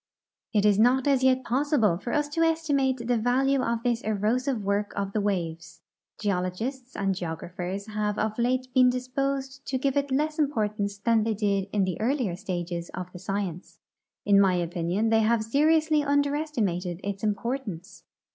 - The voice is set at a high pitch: Yes, high, 220 Hz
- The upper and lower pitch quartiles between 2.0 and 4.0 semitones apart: No, average, 5.2 semitones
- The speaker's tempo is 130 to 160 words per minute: No, average, 170 wpm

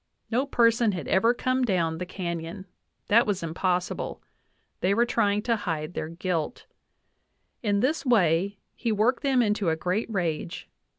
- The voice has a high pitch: Yes, high, 200 Hz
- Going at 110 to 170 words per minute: Yes, average, 155 wpm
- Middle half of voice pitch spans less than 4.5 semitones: No, average, 5.1 semitones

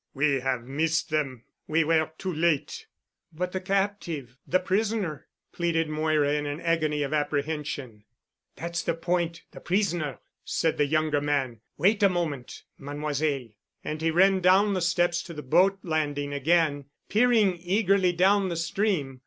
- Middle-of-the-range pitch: Yes, medium, 160 Hz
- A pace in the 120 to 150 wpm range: Yes, average, 145 wpm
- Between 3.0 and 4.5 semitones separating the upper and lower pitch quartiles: Yes, average, 3.8 semitones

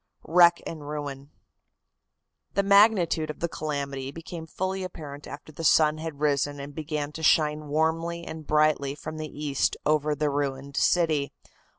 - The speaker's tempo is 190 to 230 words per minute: No, average, 155 wpm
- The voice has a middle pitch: Yes, medium, 155 Hz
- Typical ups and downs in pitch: No, narrow, 2.1 semitones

